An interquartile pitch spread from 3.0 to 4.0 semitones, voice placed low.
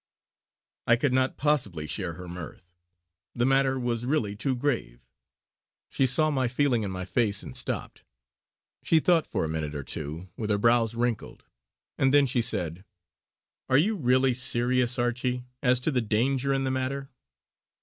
No: average, 4.5 semitones; low, 125 Hz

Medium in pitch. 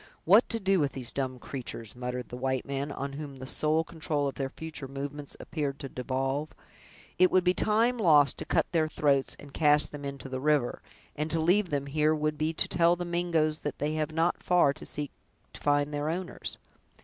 Yes: medium, 150 Hz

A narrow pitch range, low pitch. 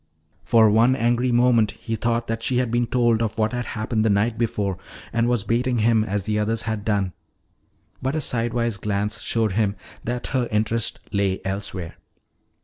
Yes: narrow, 2.2 semitones; low, 115 Hz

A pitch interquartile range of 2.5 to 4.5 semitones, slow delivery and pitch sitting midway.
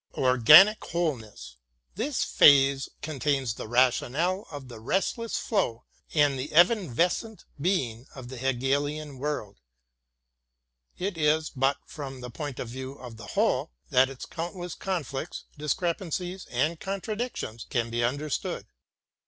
No: wide, 5.5 semitones; slow, 125 wpm; medium, 145 Hz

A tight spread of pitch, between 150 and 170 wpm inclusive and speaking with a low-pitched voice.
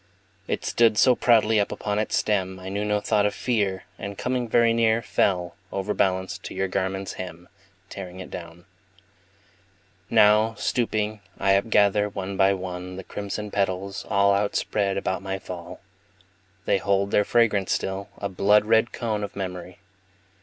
Yes: narrow, 1.9 semitones; average, 155 wpm; low, 100 Hz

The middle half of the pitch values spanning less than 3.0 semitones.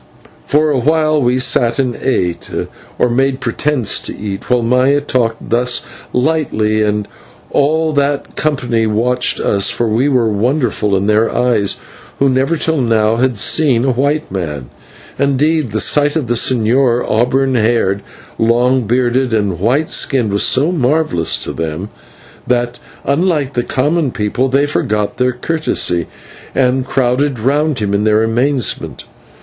No: average, 4.2 semitones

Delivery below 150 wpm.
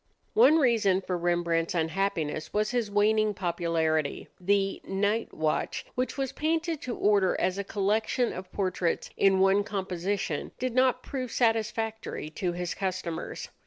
Yes: average, 140 wpm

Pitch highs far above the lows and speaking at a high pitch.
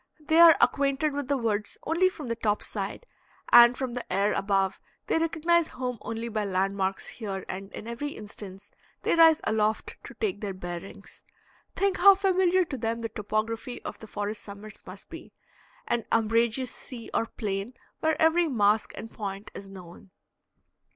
Yes: wide, 6.2 semitones; high, 230 Hz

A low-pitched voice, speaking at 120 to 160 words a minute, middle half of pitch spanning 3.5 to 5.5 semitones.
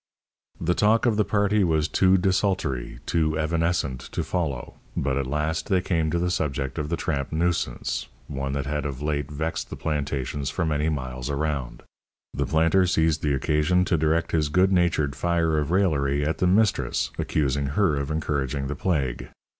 No: very low, 75 Hz; average, 180 wpm; average, 3.8 semitones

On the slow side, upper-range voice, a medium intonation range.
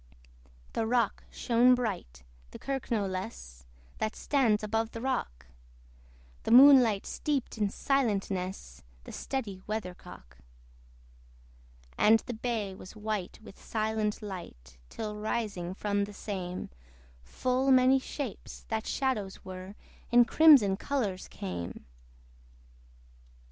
Yes: slow, 110 wpm; high, 215 Hz; average, 4.5 semitones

